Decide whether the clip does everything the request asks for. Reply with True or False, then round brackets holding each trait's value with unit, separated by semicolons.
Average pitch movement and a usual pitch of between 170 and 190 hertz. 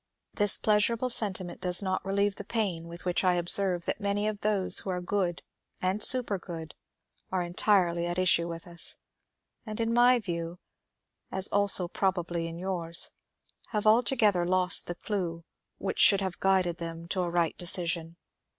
True (3.0 semitones; 185 Hz)